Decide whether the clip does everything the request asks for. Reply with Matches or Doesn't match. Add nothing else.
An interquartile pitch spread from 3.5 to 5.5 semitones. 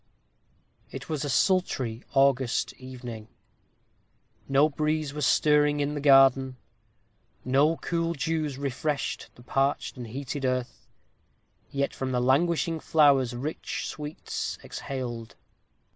Doesn't match